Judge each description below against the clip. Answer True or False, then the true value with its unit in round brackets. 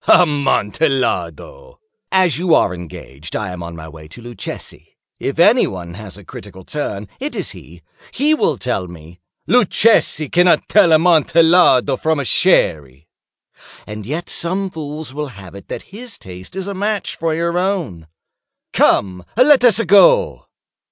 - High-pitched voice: False (150 Hz)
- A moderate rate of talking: True (150 wpm)